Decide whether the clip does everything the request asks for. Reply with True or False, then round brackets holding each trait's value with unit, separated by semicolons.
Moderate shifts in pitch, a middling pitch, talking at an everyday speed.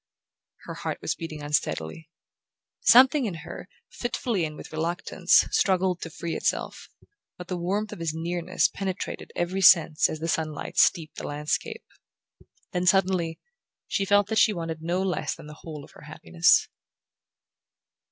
True (3.2 semitones; 170 Hz; 150 wpm)